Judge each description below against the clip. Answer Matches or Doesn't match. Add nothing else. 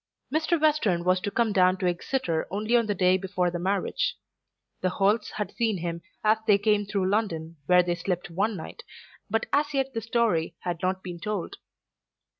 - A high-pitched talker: Matches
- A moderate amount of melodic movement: Matches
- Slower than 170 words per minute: Doesn't match